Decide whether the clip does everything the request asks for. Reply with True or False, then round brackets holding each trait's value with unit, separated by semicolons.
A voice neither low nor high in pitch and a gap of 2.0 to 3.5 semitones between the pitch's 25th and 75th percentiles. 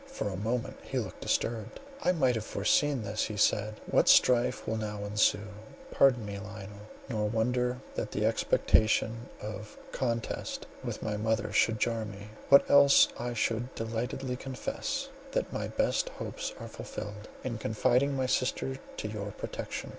False (110 Hz; 2.9 semitones)